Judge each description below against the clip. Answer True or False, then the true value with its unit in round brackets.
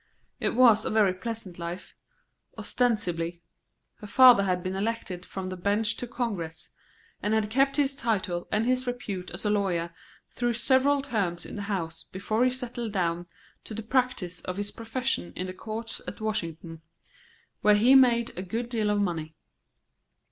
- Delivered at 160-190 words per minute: True (170 wpm)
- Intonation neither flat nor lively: True (4.6 semitones)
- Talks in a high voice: True (210 Hz)